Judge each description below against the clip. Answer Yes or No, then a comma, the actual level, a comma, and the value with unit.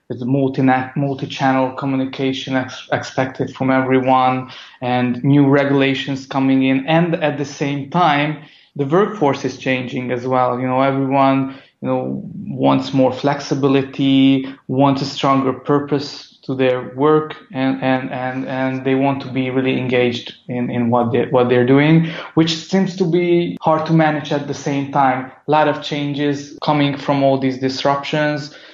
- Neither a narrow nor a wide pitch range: No, narrow, 1.8 semitones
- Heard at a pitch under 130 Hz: No, low, 135 Hz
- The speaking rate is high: No, average, 160 wpm